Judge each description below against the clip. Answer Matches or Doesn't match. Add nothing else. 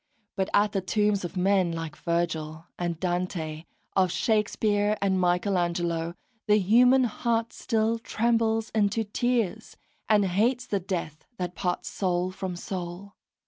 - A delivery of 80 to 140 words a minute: Matches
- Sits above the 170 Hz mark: Matches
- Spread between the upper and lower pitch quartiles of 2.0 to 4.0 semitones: Matches